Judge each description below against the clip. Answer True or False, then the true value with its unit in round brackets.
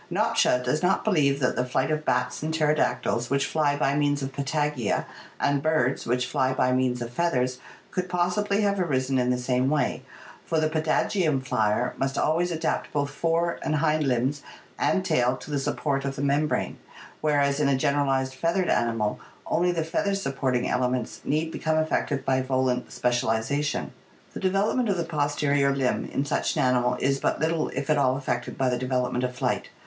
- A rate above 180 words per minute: True (190 wpm)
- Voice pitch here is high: False (140 Hz)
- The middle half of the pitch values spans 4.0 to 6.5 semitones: False (3.6 semitones)